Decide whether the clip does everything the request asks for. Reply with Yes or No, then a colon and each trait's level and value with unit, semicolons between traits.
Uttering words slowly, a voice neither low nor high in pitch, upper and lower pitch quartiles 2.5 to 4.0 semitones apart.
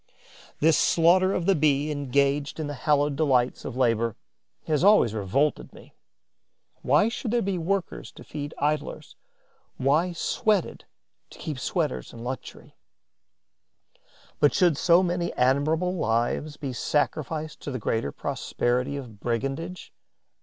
No: slow, 130 wpm; medium, 145 Hz; average, 4.6 semitones